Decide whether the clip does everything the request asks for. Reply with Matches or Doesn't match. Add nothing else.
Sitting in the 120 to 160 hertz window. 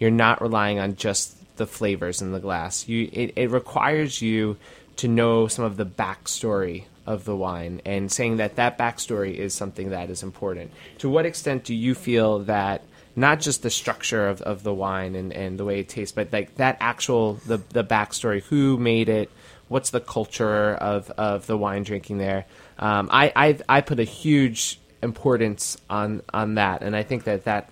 Doesn't match